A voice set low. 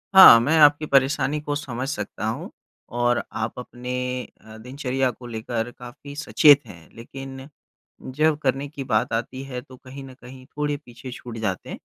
Yes: low, 130 Hz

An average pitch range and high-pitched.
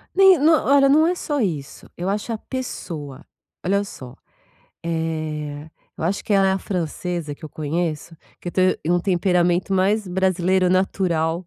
No: average, 3.6 semitones; medium, 180 Hz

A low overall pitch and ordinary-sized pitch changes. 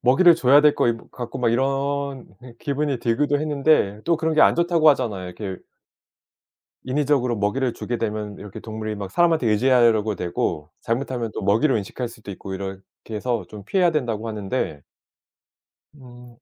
Yes: low, 120 Hz; average, 4.9 semitones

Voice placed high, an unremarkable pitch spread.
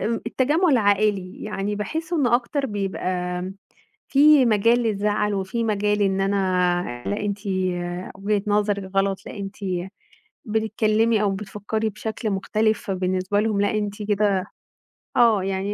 No: high, 210 Hz; narrow, 2.2 semitones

